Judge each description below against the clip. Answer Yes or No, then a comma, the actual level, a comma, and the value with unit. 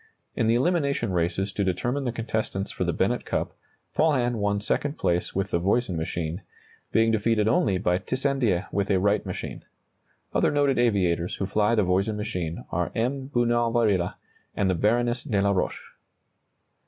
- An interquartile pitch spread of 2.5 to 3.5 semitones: No, average, 4.3 semitones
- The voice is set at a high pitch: No, low, 105 Hz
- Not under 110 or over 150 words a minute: No, average, 165 wpm